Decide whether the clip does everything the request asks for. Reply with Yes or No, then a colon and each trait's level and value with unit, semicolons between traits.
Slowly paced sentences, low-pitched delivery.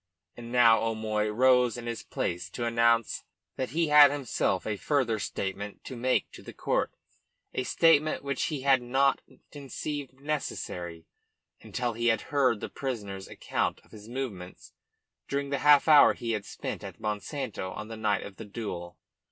No: average, 170 wpm; low, 120 Hz